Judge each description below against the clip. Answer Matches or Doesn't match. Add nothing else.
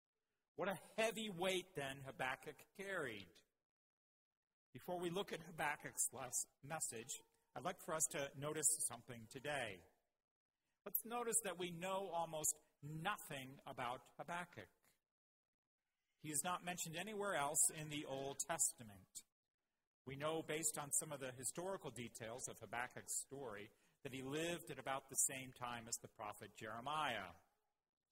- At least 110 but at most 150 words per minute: Matches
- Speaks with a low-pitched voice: Doesn't match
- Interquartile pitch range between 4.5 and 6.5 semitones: Matches